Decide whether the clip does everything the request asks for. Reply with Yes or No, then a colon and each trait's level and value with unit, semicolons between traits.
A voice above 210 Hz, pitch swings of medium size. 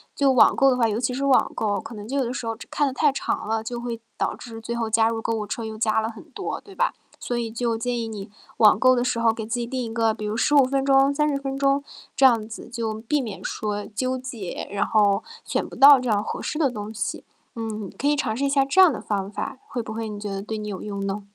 Yes: high, 230 Hz; average, 3.7 semitones